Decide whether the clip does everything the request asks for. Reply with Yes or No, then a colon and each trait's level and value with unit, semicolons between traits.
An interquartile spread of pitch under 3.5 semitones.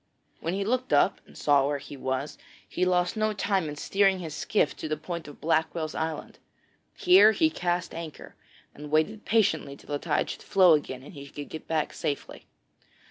No: average, 4.8 semitones